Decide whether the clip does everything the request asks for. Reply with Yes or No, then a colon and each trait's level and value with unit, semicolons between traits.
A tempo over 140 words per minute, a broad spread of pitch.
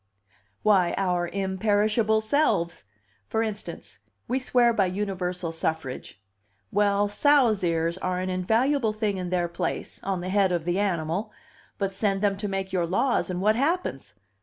No: average, 155 wpm; average, 3.2 semitones